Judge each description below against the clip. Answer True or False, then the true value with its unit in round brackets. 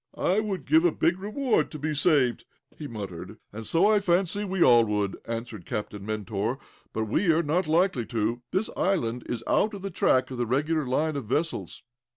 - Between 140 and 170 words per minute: False (195 wpm)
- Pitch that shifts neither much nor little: False (7.8 semitones)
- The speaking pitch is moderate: True (145 Hz)